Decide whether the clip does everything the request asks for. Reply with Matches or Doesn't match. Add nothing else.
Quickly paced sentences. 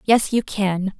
Doesn't match